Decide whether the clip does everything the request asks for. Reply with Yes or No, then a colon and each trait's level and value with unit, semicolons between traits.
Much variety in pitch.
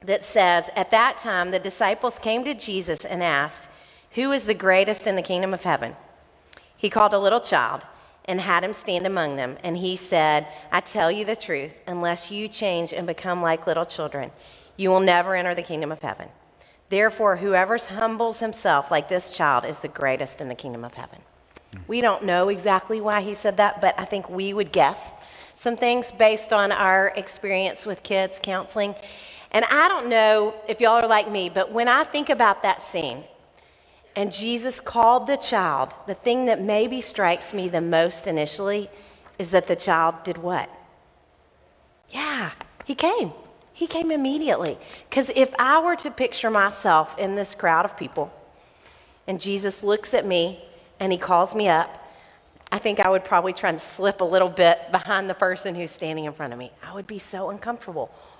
No: average, 3.8 semitones